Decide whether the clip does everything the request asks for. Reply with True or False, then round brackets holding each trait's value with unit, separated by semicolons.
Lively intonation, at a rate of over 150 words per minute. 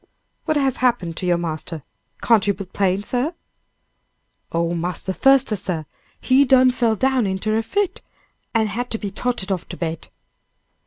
True (5.7 semitones; 165 wpm)